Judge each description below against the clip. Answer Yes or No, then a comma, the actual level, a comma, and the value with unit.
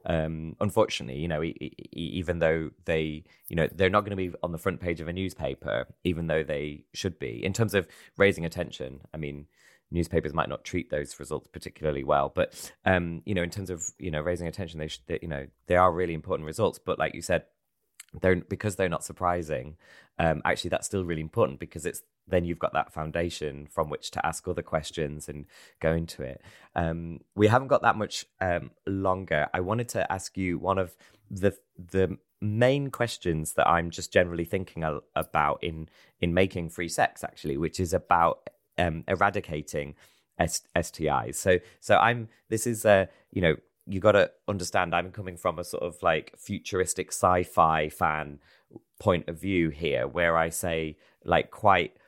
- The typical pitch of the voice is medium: No, very low, 85 Hz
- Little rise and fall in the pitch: No, average, 3.0 semitones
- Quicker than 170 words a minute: Yes, average, 190 wpm